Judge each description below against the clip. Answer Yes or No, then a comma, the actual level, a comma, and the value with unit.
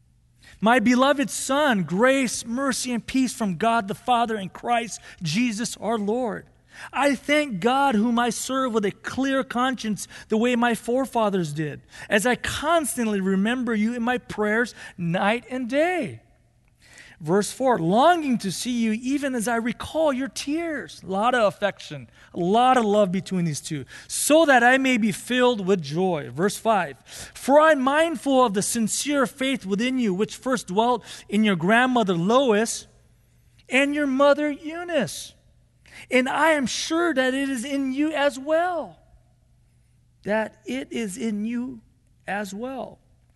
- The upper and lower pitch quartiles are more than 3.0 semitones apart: Yes, average, 4.6 semitones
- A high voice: Yes, high, 240 Hz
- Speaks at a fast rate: No, average, 160 wpm